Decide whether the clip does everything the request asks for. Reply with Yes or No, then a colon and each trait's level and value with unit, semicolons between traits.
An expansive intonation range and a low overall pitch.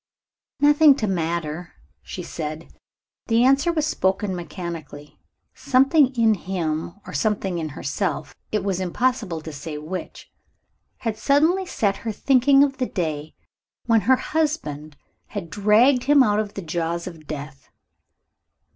No: wide, 7.7 semitones; high, 195 Hz